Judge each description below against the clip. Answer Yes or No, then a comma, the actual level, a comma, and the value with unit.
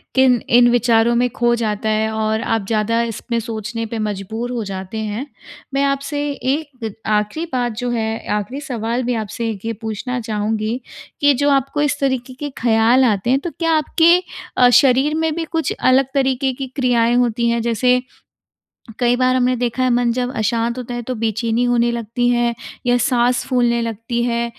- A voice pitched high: Yes, high, 240 Hz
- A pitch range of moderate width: No, narrow, 2.3 semitones